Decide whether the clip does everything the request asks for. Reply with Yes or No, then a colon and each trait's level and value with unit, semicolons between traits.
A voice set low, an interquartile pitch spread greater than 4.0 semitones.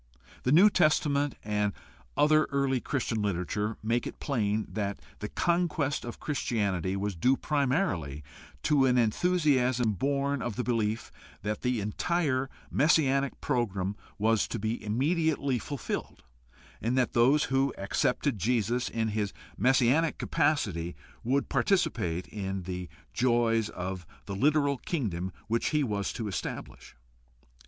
Yes: low, 120 Hz; average, 5.3 semitones